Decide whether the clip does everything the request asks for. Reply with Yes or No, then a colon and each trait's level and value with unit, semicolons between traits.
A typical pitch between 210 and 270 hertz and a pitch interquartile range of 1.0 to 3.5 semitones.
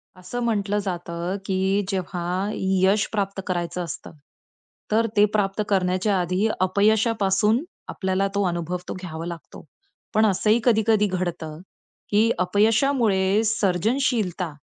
No: high, 195 Hz; average, 2.8 semitones